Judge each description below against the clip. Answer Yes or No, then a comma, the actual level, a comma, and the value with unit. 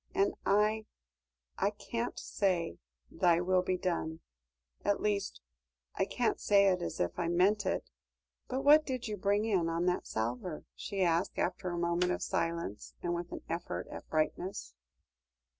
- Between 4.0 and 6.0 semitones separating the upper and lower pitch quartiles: No, average, 3.2 semitones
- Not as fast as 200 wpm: Yes, average, 160 wpm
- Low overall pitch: No, medium, 185 Hz